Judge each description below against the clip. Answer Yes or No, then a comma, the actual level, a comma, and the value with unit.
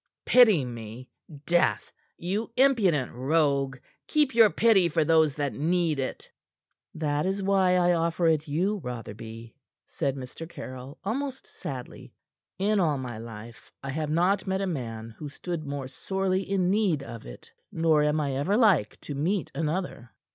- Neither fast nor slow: Yes, average, 155 wpm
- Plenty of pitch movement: Yes, wide, 6.0 semitones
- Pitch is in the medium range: Yes, medium, 160 Hz